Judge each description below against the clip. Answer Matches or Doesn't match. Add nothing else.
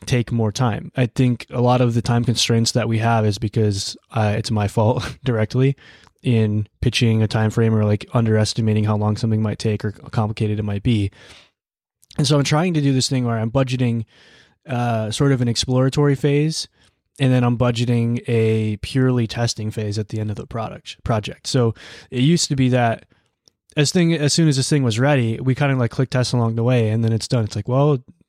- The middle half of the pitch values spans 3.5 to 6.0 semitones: Doesn't match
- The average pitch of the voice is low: Matches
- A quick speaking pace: Matches